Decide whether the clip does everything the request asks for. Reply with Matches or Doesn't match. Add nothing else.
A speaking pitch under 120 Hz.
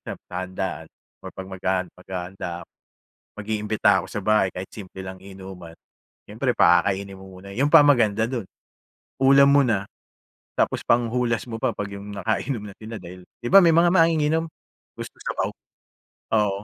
Matches